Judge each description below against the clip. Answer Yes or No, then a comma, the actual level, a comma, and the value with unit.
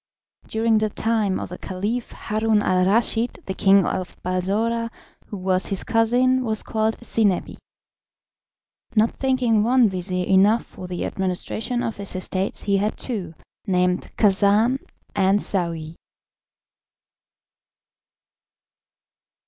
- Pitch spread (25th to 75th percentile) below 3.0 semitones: No, average, 3.4 semitones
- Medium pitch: No, high, 205 Hz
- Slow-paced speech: Yes, slow, 115 wpm